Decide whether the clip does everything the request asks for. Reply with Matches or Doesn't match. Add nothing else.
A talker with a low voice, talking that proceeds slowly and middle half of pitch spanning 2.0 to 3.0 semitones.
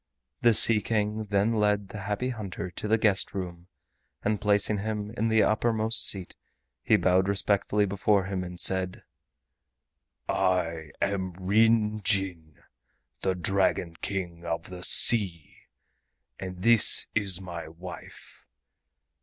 Matches